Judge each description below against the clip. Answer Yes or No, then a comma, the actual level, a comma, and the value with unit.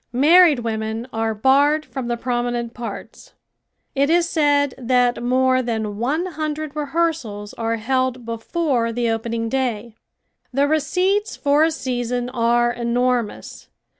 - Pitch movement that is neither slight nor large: Yes, average, 3.9 semitones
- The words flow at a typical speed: No, slow, 130 wpm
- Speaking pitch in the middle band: No, very high, 250 Hz